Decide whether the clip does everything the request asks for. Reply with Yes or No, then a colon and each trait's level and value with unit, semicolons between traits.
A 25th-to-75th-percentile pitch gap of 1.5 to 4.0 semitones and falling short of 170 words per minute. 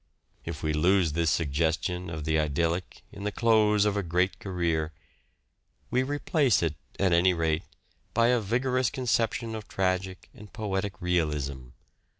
No: average, 4.6 semitones; average, 150 wpm